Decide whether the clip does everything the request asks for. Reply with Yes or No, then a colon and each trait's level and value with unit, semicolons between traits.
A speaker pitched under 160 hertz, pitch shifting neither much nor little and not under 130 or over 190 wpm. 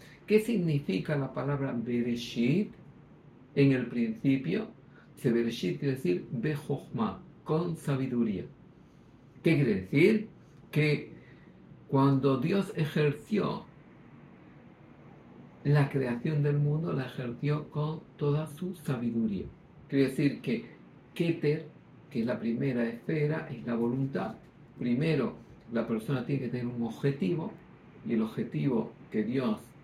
No: medium, 140 Hz; average, 4.2 semitones; slow, 115 wpm